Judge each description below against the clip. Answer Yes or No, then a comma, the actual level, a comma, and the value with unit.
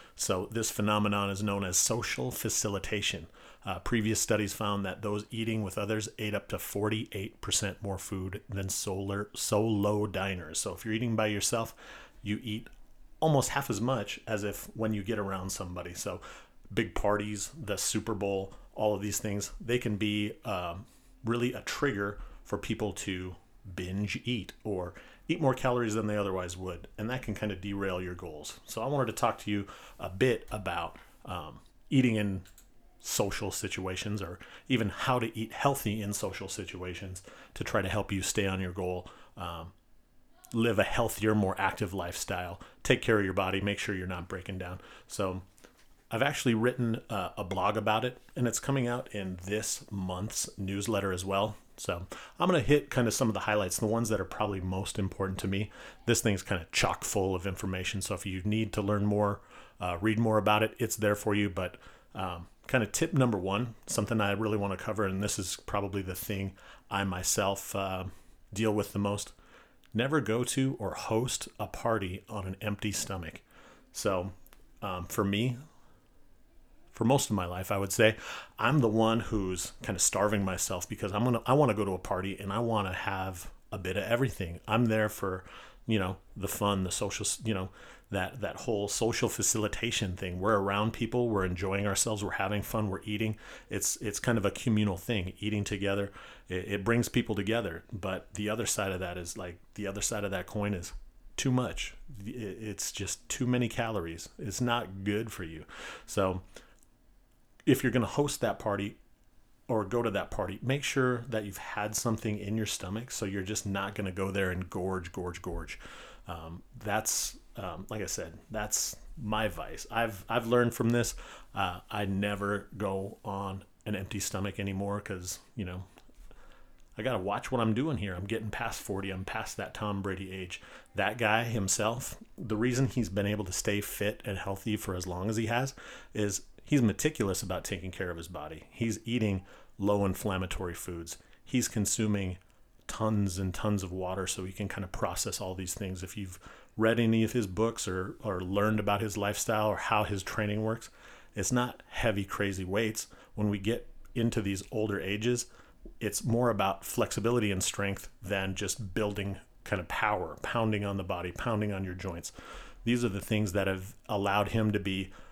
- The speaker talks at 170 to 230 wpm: Yes, average, 190 wpm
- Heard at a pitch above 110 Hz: No, low, 105 Hz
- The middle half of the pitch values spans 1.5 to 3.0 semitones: Yes, narrow, 2.6 semitones